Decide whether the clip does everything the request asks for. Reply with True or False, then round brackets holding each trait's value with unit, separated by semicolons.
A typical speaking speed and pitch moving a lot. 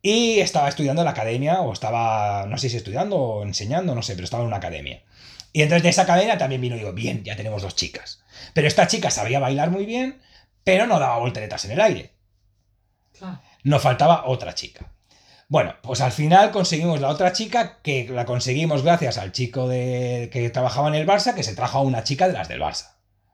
False (215 wpm; 7.7 semitones)